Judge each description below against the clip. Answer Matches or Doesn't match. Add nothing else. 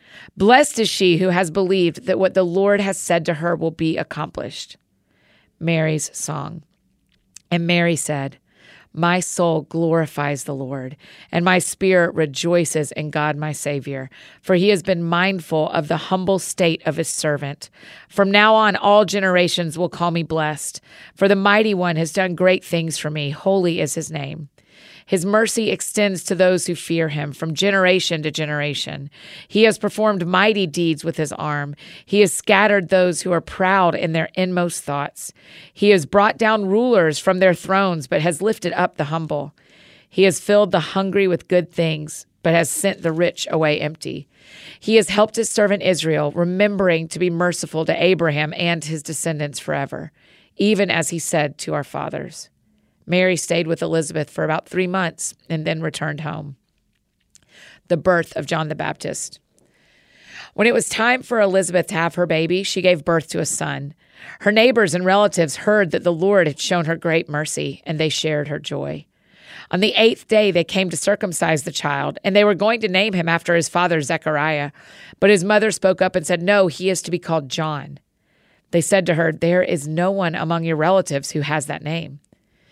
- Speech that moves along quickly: Doesn't match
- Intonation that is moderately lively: Matches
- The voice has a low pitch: Doesn't match